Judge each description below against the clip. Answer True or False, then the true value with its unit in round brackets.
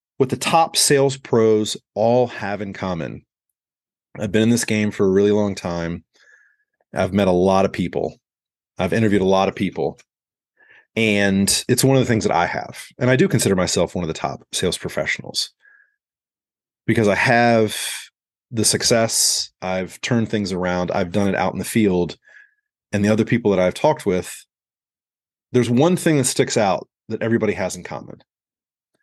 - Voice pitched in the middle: False (105 Hz)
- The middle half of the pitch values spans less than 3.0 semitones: False (4.2 semitones)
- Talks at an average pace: True (180 wpm)